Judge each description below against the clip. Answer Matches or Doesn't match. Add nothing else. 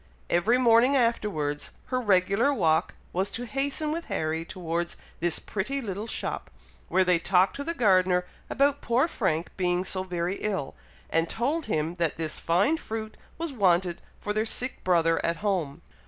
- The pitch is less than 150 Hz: Doesn't match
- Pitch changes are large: Matches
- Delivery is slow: Doesn't match